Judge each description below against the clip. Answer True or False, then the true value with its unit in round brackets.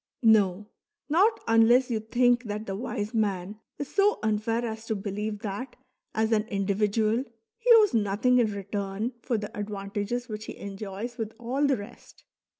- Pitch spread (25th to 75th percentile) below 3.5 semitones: True (3.0 semitones)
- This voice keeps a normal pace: True (160 wpm)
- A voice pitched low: False (220 Hz)